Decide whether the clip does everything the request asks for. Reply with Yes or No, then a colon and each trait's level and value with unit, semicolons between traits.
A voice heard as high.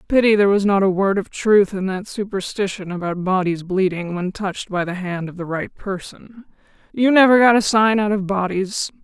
Yes: high, 195 Hz